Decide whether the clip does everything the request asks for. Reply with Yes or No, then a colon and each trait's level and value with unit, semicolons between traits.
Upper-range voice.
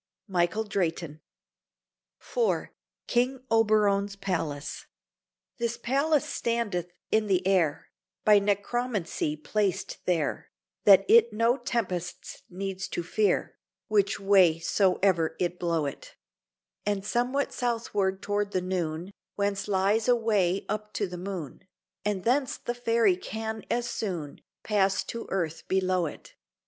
Yes: high, 200 Hz